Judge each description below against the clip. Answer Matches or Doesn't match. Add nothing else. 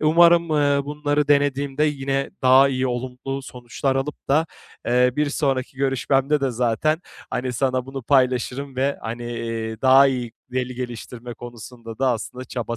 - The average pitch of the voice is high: Doesn't match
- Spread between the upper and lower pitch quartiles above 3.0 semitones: Doesn't match